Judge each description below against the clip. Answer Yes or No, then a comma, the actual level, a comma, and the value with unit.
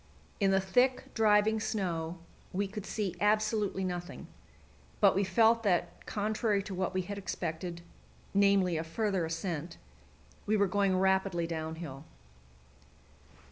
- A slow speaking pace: Yes, slow, 130 wpm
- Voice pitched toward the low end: No, high, 190 Hz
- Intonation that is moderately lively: Yes, average, 3.0 semitones